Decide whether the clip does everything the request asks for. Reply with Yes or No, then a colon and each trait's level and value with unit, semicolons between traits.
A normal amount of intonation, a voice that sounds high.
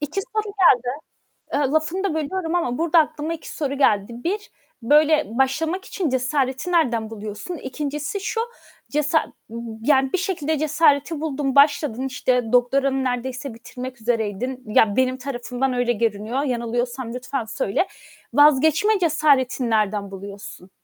Yes: average, 4.3 semitones; very high, 270 Hz